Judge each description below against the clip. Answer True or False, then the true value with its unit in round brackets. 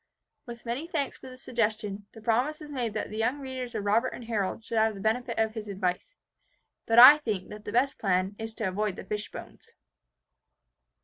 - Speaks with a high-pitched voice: True (225 Hz)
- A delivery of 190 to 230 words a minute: True (205 wpm)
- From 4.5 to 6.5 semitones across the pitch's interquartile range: False (3.3 semitones)